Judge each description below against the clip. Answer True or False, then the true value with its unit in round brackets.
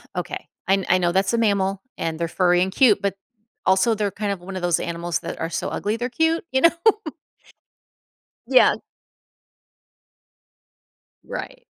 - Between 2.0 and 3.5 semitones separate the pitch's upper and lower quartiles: False (4.0 semitones)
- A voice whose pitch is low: False (195 Hz)